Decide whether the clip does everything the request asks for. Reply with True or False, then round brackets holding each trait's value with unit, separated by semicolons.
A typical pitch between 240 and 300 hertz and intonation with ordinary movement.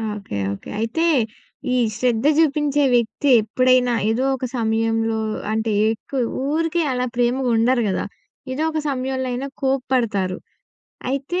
True (250 Hz; 3.2 semitones)